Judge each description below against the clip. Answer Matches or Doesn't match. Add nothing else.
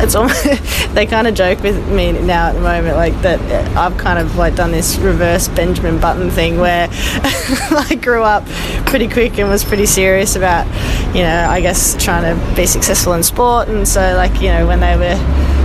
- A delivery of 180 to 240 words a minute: Matches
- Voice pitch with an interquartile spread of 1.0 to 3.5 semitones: Doesn't match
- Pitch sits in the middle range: Doesn't match